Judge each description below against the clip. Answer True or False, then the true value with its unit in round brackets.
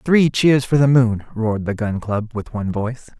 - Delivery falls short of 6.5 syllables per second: True (5.0 syllables/s)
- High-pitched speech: False (120 Hz)